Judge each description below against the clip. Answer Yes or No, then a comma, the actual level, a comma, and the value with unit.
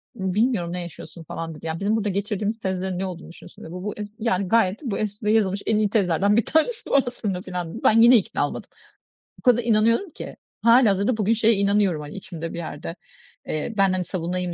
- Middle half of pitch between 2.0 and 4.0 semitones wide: Yes, average, 3.5 semitones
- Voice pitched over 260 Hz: No, high, 200 Hz